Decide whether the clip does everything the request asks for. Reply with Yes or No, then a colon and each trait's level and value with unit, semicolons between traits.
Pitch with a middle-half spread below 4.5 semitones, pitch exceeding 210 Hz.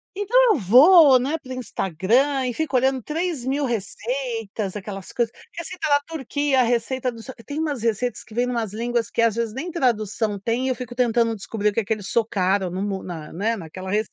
Yes: average, 4.1 semitones; high, 235 Hz